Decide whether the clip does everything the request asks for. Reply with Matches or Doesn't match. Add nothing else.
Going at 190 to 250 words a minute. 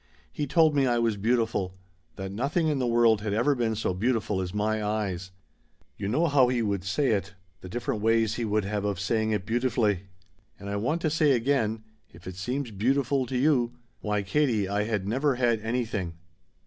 Matches